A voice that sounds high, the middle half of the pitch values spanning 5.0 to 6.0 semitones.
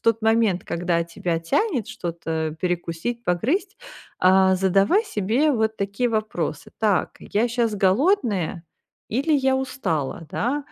Yes: high, 210 Hz; wide, 5.6 semitones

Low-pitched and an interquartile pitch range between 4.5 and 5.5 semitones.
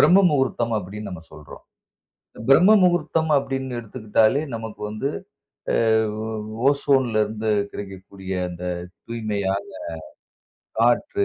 Yes: low, 110 Hz; average, 5.2 semitones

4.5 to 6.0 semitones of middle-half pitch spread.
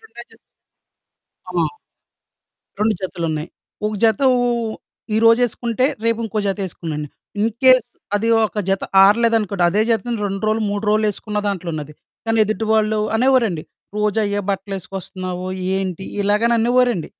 No: average, 3.0 semitones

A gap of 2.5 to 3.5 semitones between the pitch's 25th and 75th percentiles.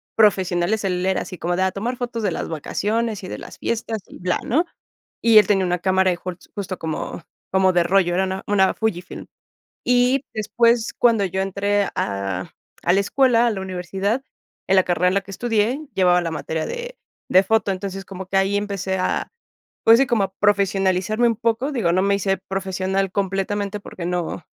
Yes: average, 3.0 semitones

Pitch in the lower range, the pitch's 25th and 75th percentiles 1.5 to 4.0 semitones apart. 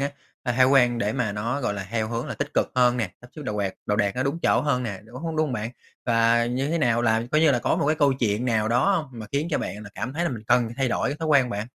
Yes: low, 120 Hz; average, 3.7 semitones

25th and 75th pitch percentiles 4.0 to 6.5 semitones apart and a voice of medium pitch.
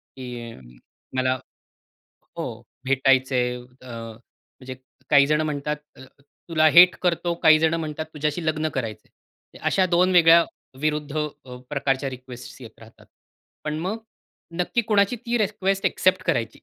Yes: average, 4.7 semitones; medium, 150 Hz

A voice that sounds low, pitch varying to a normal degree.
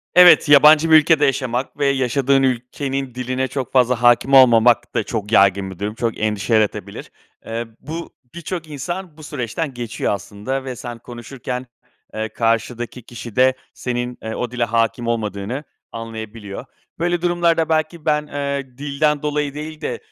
Yes: low, 125 Hz; average, 4.1 semitones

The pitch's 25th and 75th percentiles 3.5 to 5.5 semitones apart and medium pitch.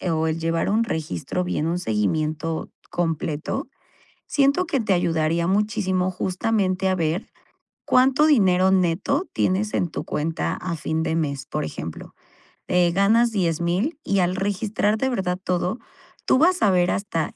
Yes: average, 4.2 semitones; medium, 180 Hz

